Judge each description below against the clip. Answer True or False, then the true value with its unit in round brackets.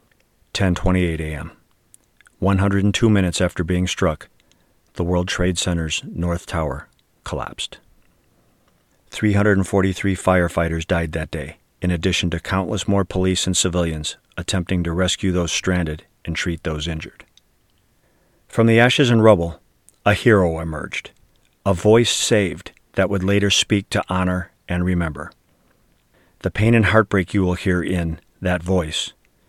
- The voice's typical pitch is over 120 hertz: False (90 Hz)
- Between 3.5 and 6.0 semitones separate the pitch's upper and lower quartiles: False (2.8 semitones)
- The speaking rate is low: True (130 wpm)